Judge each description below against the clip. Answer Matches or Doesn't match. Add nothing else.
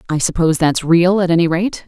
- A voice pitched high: Doesn't match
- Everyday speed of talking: Doesn't match